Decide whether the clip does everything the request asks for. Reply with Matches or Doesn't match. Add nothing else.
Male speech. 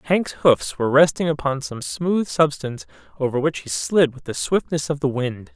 Matches